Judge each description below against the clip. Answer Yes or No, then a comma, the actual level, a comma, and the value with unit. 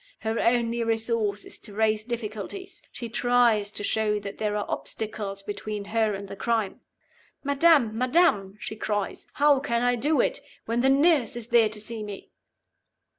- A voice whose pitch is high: Yes, high, 225 Hz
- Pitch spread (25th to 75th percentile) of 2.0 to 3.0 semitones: Yes, narrow, 2.6 semitones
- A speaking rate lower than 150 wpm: No, average, 170 wpm